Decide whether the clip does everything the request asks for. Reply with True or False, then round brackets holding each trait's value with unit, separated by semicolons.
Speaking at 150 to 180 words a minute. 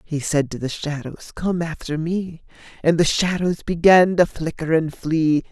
True (175 wpm)